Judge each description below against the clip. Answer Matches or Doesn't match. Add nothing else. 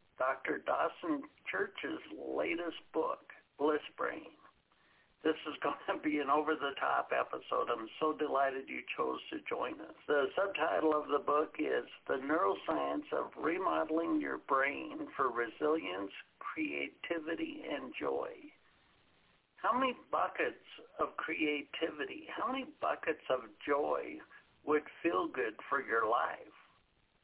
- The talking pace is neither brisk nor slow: Doesn't match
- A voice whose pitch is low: Doesn't match